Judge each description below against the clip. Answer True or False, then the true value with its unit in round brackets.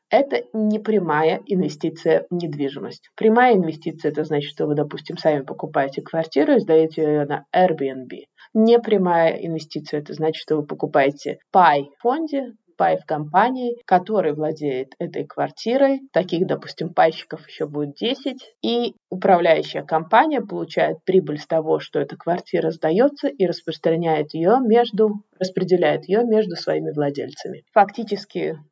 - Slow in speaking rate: False (135 wpm)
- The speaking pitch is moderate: True (170 Hz)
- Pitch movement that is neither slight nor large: False (6.0 semitones)